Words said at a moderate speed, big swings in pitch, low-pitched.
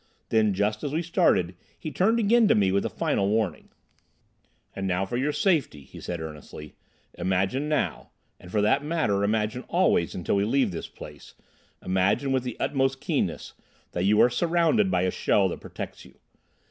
Yes: average, 170 wpm; wide, 7.8 semitones; low, 110 Hz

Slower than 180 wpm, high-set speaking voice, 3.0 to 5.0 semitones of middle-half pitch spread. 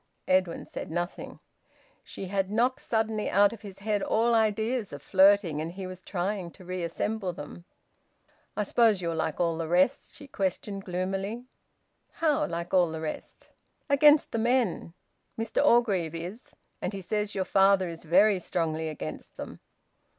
Yes: average, 160 wpm; high, 195 Hz; average, 4.0 semitones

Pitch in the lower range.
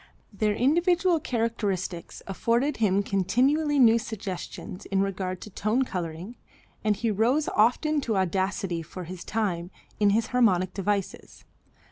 No: high, 210 Hz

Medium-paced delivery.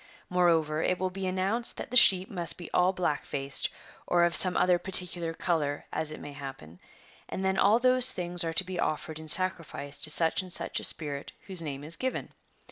No: fast, 210 wpm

